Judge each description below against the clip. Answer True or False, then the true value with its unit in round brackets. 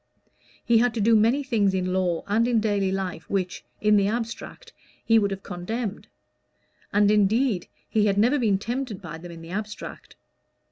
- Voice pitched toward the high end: True (210 Hz)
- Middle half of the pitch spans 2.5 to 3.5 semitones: True (3.1 semitones)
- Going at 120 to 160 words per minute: False (180 wpm)